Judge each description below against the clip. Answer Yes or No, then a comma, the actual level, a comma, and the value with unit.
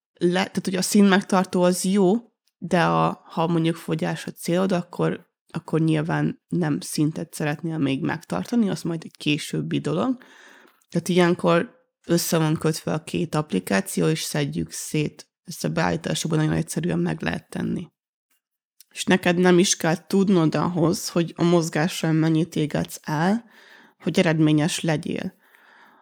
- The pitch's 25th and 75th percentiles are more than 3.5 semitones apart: No, average, 2.9 semitones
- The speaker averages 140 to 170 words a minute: Yes, average, 145 wpm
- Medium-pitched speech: Yes, medium, 170 Hz